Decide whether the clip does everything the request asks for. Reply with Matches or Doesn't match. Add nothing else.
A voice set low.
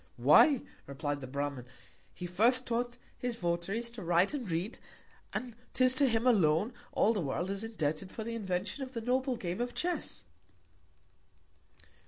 Doesn't match